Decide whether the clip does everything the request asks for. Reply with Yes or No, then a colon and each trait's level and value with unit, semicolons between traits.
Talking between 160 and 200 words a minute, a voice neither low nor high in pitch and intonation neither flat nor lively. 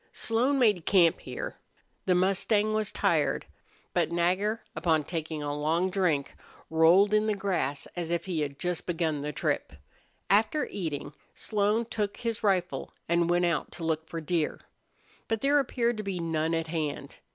Yes: average, 165 wpm; medium, 175 Hz; average, 4.5 semitones